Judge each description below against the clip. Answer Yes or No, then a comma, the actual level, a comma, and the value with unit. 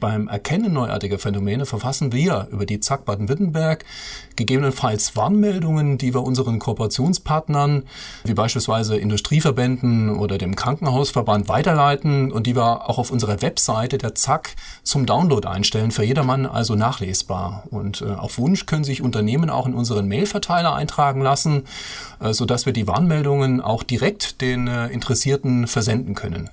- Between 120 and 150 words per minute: Yes, average, 135 wpm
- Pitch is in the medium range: No, low, 125 Hz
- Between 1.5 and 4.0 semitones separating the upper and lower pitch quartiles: No, average, 4.8 semitones